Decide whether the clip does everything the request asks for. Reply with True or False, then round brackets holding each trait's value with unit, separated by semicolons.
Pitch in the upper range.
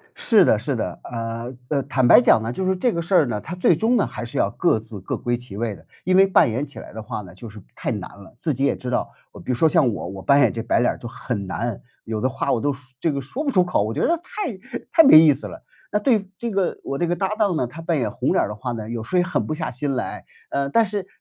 False (140 Hz)